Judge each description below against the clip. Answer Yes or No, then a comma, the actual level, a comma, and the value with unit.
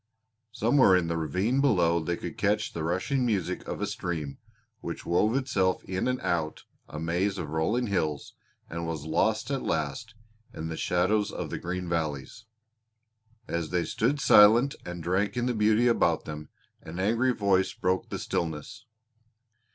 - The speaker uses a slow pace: No, average, 165 wpm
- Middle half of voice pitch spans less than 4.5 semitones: No, average, 5.0 semitones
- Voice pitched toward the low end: Yes, very low, 95 Hz